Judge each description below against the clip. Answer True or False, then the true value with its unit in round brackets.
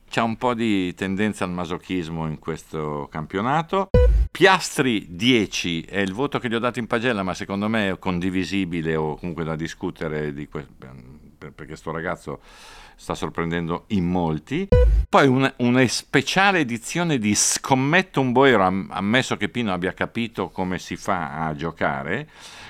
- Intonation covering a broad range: True (6.5 semitones)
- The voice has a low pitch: True (95 Hz)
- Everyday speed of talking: True (155 wpm)